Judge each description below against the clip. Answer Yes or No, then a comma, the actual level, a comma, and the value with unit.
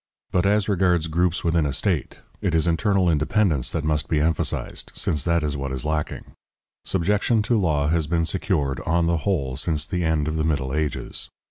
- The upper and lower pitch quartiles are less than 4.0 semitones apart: Yes, average, 3.0 semitones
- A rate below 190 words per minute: No, average, 195 wpm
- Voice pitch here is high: No, very low, 80 Hz